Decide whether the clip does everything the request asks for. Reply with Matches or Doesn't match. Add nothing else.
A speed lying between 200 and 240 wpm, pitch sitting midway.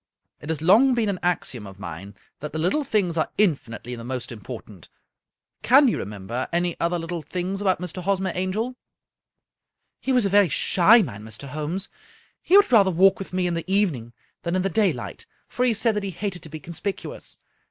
Matches